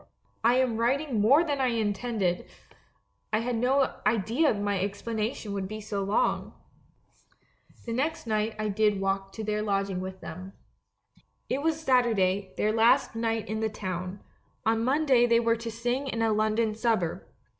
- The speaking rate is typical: Yes, average, 165 wpm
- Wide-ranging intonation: No, average, 3.0 semitones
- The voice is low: No, high, 220 Hz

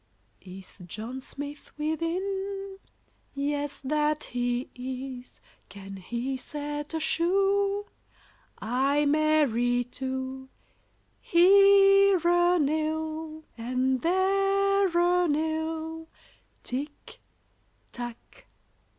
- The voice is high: Yes, very high, 305 Hz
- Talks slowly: Yes, slow, 85 wpm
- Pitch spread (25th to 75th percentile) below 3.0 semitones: No, average, 5.3 semitones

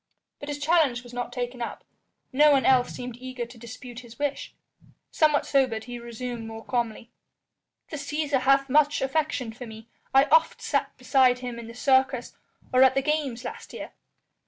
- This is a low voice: No, very high, 255 Hz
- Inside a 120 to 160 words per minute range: No, average, 180 wpm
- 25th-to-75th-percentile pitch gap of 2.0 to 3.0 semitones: Yes, average, 2.7 semitones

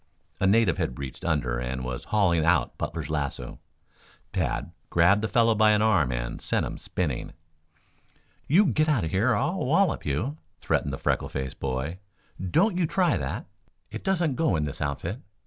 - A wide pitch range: Yes, wide, 8.5 semitones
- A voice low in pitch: Yes, very low, 90 Hz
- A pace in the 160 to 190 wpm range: Yes, average, 180 wpm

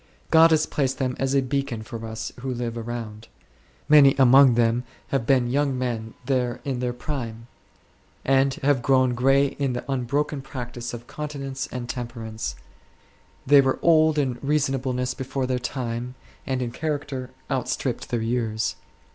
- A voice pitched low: Yes, low, 130 Hz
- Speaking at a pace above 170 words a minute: No, average, 155 wpm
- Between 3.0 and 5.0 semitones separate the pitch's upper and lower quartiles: No, narrow, 2.4 semitones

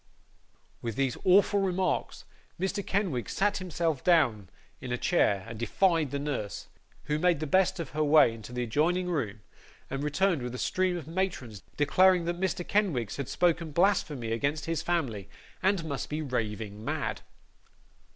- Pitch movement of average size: No, wide, 6.5 semitones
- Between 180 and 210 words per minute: No, average, 160 wpm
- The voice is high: No, medium, 155 Hz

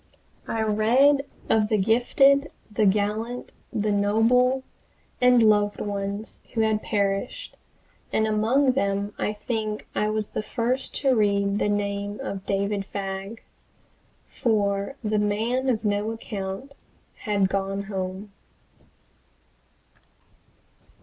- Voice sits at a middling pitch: No, high, 210 Hz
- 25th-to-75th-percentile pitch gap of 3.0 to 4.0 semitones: No, narrow, 2.4 semitones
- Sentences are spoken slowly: Yes, slow, 115 wpm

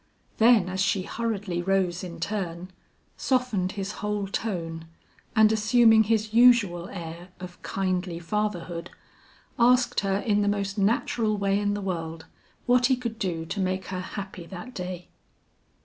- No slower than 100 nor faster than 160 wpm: Yes, average, 150 wpm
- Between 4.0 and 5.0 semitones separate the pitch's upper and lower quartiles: No, average, 3.4 semitones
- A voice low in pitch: No, high, 195 Hz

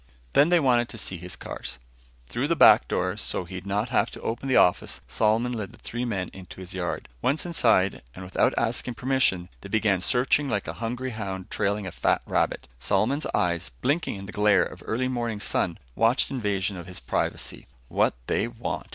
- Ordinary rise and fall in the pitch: Yes, average, 4.6 semitones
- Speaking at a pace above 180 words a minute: Yes, average, 195 wpm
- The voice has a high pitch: No, low, 110 Hz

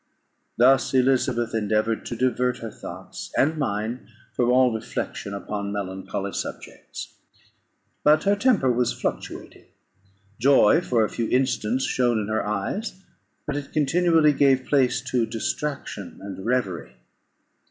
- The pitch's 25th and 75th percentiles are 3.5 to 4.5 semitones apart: Yes, average, 4.0 semitones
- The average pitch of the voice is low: Yes, low, 125 Hz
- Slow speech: Yes, slow, 130 wpm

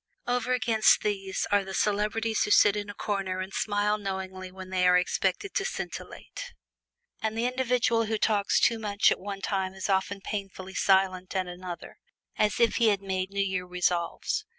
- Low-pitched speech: No, high, 200 Hz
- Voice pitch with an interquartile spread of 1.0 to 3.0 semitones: Yes, narrow, 2.5 semitones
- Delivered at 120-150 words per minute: No, average, 180 wpm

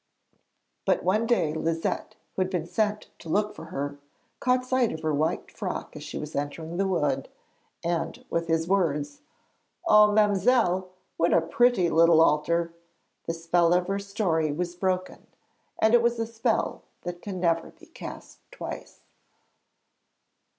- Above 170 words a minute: No, average, 155 wpm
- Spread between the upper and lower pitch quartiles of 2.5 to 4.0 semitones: No, average, 4.4 semitones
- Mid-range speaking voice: Yes, medium, 175 Hz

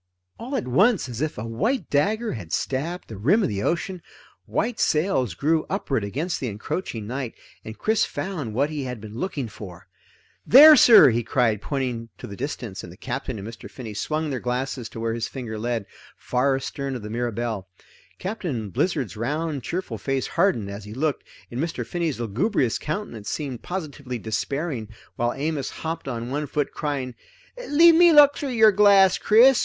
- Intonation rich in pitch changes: Yes, wide, 7.4 semitones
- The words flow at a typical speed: Yes, average, 180 wpm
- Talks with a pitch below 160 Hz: Yes, low, 135 Hz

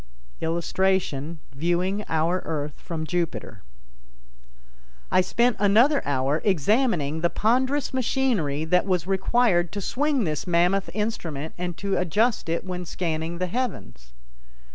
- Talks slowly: Yes, slow, 120 wpm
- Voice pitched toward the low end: No, medium, 180 Hz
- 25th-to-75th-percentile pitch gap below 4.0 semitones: No, average, 4.6 semitones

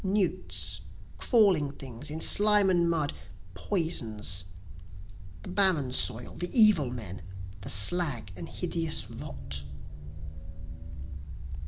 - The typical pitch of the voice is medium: Yes, medium, 155 Hz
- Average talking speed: No, slow, 100 wpm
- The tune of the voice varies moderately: No, wide, 8.3 semitones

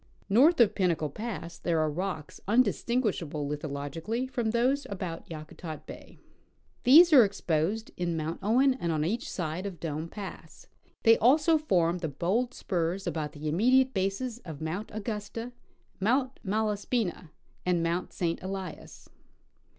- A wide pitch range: Yes, wide, 6.2 semitones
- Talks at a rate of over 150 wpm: No, average, 145 wpm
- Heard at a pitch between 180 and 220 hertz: Yes, high, 190 Hz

